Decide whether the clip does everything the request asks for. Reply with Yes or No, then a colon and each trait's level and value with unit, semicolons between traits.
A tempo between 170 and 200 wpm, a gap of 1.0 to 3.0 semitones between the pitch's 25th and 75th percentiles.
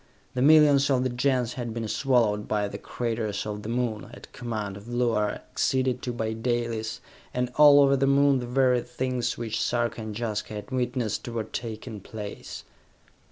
Yes: average, 175 wpm; narrow, 2.6 semitones